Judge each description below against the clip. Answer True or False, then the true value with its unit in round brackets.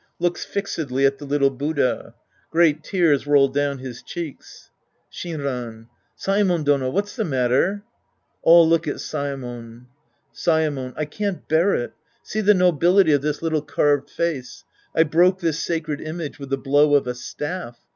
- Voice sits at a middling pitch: True (150 Hz)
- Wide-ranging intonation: False (3.8 semitones)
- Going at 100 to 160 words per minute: True (155 wpm)